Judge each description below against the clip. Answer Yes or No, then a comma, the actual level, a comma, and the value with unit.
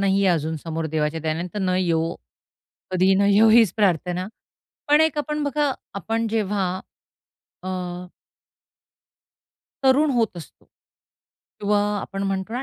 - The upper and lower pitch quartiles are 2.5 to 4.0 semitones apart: No, average, 4.5 semitones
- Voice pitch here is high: Yes, high, 195 Hz